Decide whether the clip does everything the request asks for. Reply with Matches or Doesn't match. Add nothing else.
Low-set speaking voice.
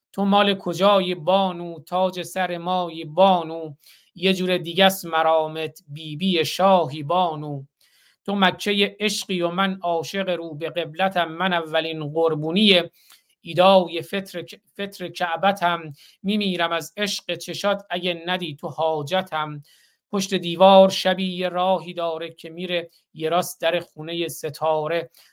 Doesn't match